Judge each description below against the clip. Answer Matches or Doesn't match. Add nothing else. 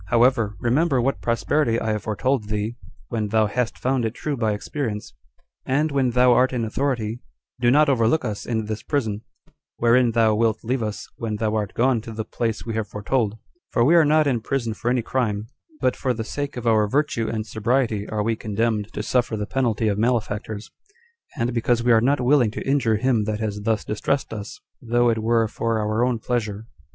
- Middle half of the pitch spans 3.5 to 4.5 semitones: Doesn't match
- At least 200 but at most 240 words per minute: Matches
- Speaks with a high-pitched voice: Doesn't match